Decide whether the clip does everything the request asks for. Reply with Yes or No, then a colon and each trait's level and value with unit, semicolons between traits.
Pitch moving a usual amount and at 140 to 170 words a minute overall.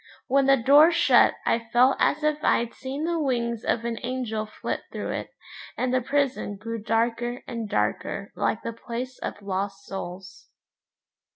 Yes: average, 3.2 semitones; average, 165 wpm